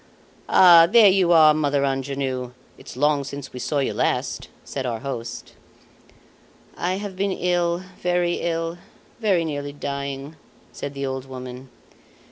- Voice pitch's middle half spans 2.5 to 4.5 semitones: Yes, average, 4.2 semitones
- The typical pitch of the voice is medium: Yes, medium, 145 Hz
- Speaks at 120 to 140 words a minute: Yes, slow, 135 wpm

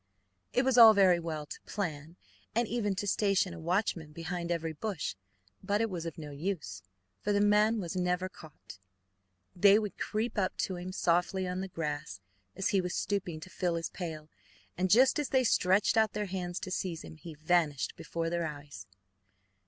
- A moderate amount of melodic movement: Yes, average, 3.6 semitones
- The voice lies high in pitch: No, medium, 180 Hz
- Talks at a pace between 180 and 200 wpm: Yes, average, 190 wpm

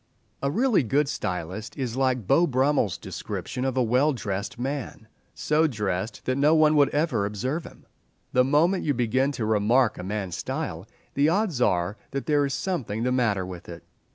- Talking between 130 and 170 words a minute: No, average, 180 wpm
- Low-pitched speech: Yes, low, 130 Hz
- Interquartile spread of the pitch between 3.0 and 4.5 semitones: No, wide, 5.5 semitones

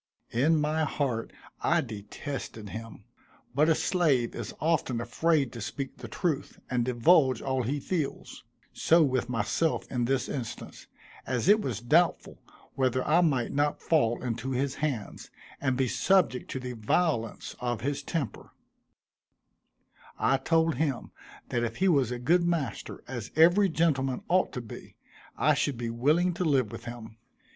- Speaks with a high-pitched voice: No, low, 135 Hz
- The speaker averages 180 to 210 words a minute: No, average, 155 wpm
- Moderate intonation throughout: Yes, average, 4.9 semitones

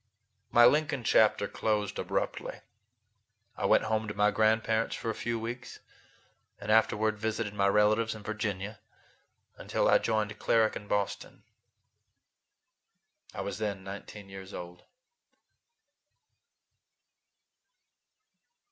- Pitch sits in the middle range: No, low, 110 Hz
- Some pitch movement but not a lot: No, narrow, 1.4 semitones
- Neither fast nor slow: No, slow, 110 wpm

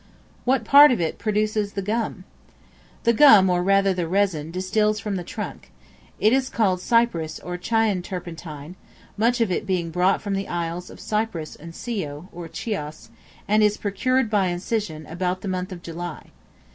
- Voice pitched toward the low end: No, high, 190 Hz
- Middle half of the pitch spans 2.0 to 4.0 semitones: Yes, average, 3.6 semitones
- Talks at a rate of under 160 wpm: No, average, 170 wpm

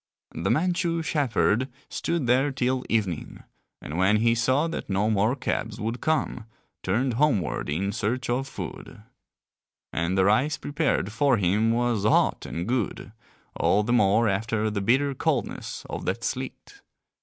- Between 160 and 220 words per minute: No, average, 150 wpm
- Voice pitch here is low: Yes, low, 115 Hz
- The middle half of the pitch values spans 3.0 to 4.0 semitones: No, average, 4.4 semitones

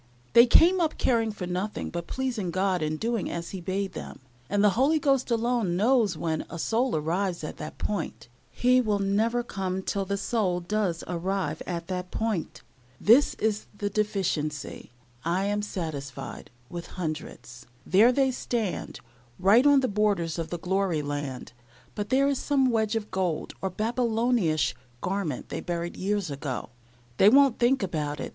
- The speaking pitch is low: No, high, 195 Hz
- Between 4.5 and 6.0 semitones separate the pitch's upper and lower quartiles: Yes, average, 5.0 semitones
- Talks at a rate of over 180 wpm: No, average, 170 wpm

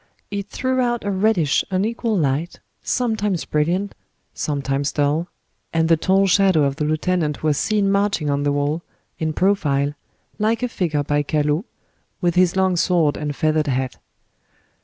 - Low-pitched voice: No, medium, 170 Hz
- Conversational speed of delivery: Yes, average, 155 wpm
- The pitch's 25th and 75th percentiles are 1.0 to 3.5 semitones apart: No, average, 5.1 semitones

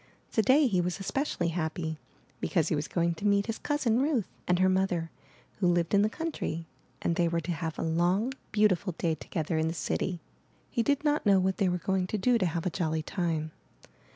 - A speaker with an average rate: No, fast, 210 wpm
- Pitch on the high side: No, medium, 180 Hz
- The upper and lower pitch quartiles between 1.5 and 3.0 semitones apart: No, average, 4.1 semitones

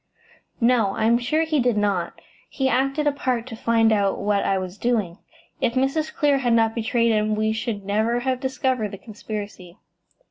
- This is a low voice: No, high, 230 Hz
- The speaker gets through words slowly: No, average, 185 wpm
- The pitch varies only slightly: No, average, 3.7 semitones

